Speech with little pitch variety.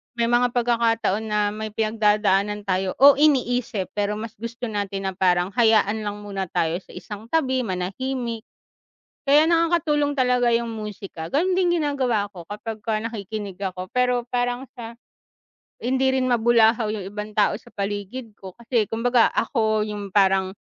No: average, 3.3 semitones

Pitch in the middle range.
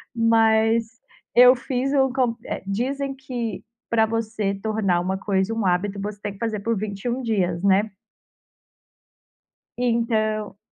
No: high, 220 Hz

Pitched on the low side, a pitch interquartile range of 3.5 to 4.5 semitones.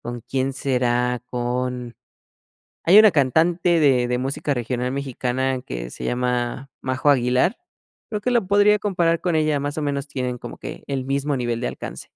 Yes: low, 130 Hz; average, 3.8 semitones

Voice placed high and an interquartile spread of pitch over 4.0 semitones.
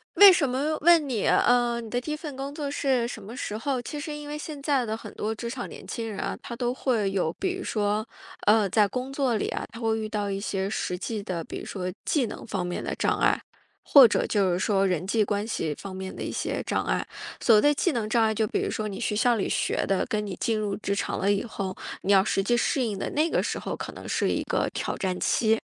Yes: high, 220 Hz; average, 4.6 semitones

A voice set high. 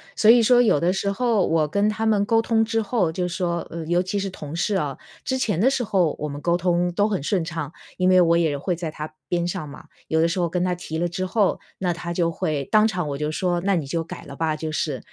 No: medium, 175 Hz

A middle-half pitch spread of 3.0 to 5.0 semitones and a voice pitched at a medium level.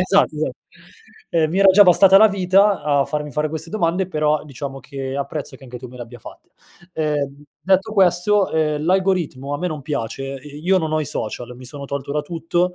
Yes: average, 4.5 semitones; medium, 155 Hz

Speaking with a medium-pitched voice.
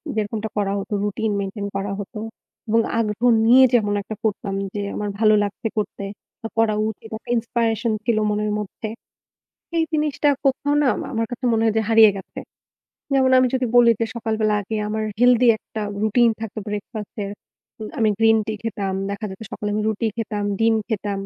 No: high, 220 Hz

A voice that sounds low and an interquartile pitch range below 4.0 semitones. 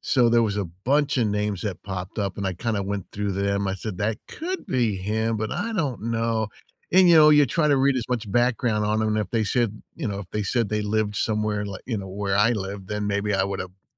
Yes: low, 105 Hz; average, 2.9 semitones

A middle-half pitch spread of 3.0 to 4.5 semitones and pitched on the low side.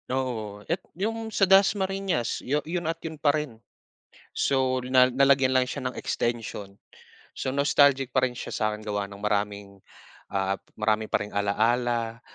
No: average, 5.2 semitones; low, 125 Hz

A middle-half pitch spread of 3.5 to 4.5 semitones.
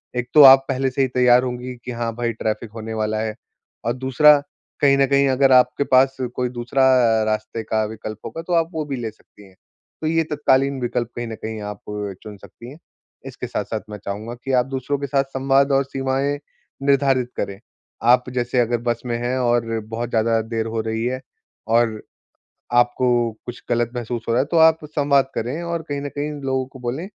No: average, 2.8 semitones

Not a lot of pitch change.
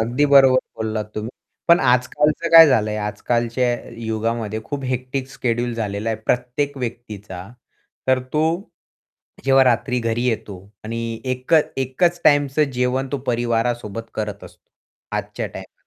No: average, 3.0 semitones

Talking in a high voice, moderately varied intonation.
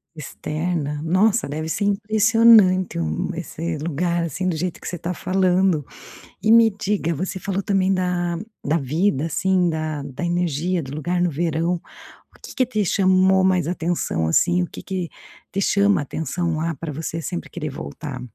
No: medium, 175 Hz; average, 3.2 semitones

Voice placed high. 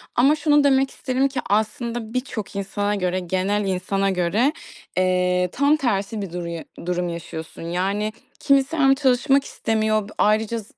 Yes: high, 210 Hz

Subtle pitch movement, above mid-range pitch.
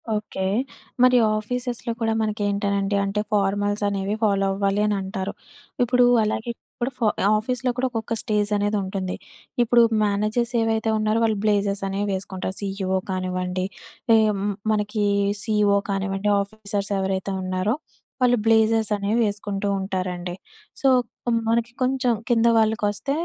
Yes: narrow, 2.2 semitones; high, 205 Hz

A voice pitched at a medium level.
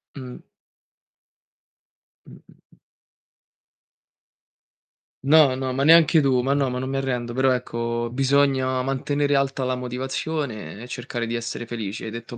No: low, 130 Hz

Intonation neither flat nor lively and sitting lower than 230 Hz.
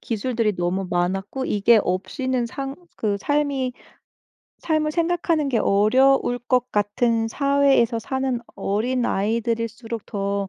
No: average, 4.4 semitones; high, 235 Hz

